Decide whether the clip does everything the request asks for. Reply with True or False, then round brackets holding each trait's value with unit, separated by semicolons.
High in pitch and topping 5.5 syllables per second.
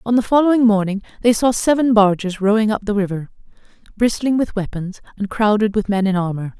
True (210 Hz; 5.8 syllables/s)